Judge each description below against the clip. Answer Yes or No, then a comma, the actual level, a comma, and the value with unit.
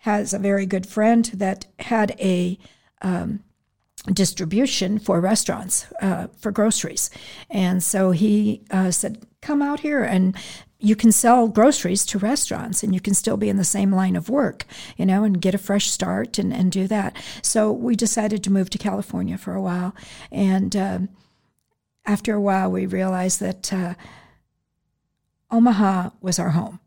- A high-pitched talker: Yes, high, 200 Hz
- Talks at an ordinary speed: Yes, average, 170 wpm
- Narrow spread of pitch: Yes, narrow, 2.2 semitones